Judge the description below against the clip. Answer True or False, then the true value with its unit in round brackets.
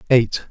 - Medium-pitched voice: False (115 Hz)